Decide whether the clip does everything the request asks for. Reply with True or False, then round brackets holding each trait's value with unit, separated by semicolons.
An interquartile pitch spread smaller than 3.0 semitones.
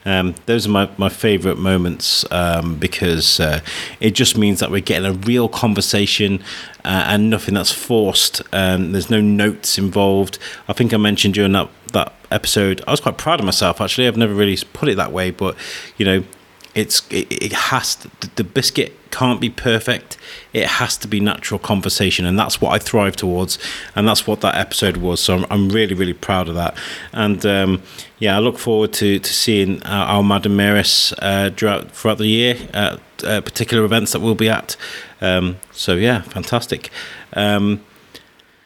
True (2.5 semitones)